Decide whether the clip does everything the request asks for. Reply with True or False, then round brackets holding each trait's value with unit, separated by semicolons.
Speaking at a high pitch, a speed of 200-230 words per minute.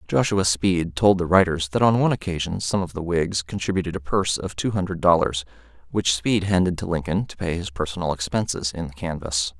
False (90 Hz; 205 wpm)